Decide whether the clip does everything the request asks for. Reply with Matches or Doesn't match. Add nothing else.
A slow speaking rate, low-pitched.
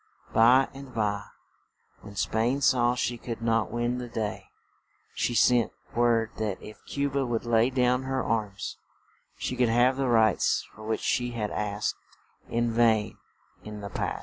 Doesn't match